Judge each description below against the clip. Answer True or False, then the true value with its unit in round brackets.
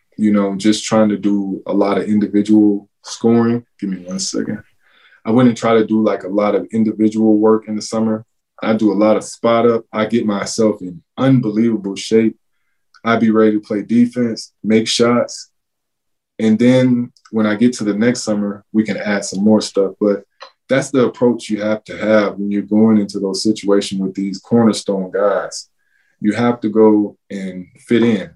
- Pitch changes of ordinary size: False (1.8 semitones)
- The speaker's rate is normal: True (190 wpm)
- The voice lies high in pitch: False (110 Hz)